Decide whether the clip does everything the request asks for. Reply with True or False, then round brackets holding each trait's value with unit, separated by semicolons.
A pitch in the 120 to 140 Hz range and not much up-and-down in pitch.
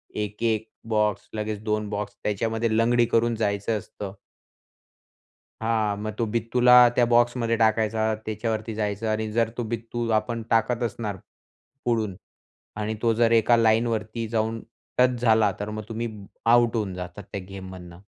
False (110 Hz; 1.6 semitones)